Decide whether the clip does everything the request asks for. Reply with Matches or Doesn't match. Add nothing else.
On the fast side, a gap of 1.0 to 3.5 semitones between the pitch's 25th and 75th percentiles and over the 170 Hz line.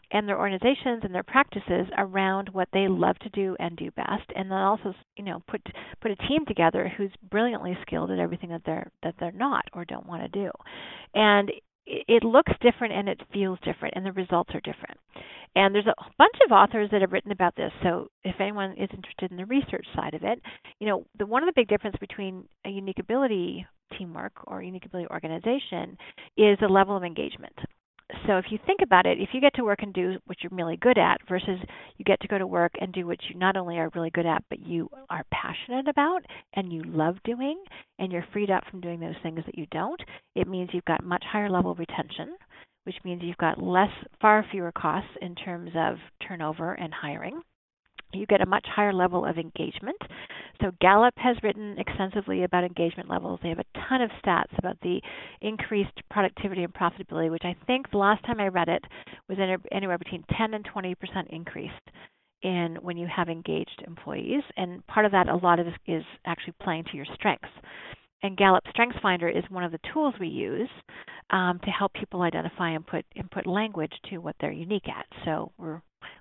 Matches